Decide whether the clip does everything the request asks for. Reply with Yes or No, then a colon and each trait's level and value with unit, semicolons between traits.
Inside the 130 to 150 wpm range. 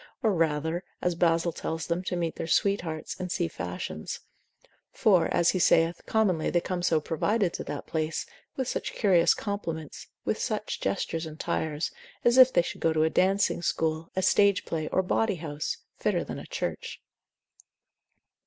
No: average, 170 wpm